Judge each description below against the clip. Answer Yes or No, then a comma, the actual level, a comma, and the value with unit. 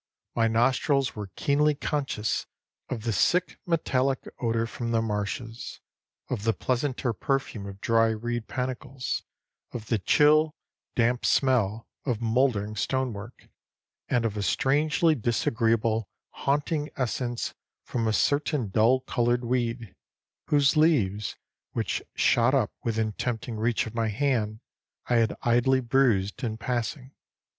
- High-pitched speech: No, low, 120 Hz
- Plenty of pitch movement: No, average, 3.1 semitones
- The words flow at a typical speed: No, slow, 130 wpm